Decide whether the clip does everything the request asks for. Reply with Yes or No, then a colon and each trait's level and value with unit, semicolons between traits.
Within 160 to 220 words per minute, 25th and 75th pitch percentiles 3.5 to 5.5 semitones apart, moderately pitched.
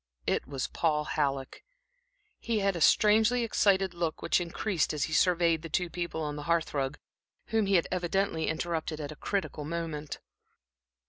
Yes: average, 170 wpm; average, 3.8 semitones; medium, 170 Hz